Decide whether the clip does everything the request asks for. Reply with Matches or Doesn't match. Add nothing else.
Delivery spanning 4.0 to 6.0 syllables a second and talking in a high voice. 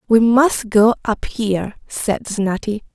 Doesn't match